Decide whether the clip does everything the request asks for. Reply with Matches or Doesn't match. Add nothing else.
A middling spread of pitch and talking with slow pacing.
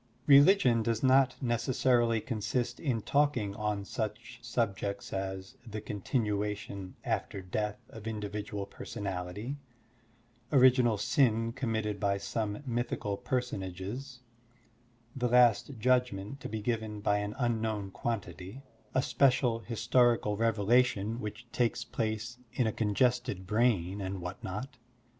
Matches